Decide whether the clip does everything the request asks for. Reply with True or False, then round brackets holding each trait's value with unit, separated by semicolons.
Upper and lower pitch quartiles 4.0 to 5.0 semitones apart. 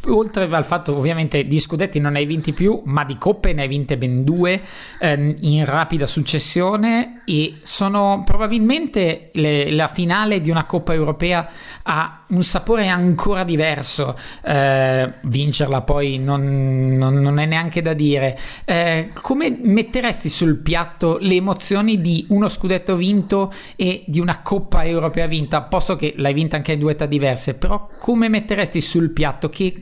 True (4.4 semitones)